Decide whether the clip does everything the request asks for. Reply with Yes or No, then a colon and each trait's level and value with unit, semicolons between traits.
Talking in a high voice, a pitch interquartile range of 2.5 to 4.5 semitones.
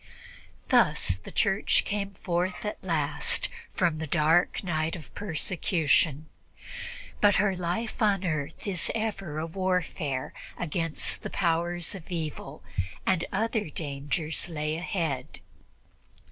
No: medium, 170 Hz; average, 3.6 semitones